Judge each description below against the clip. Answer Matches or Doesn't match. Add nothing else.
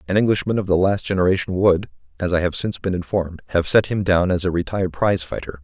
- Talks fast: Matches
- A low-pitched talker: Matches